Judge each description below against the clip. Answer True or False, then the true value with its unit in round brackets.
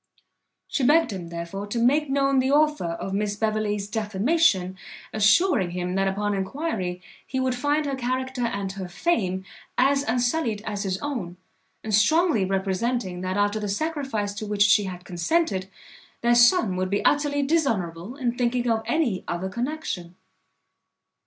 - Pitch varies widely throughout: True (6.0 semitones)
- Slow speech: False (155 wpm)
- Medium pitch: False (215 Hz)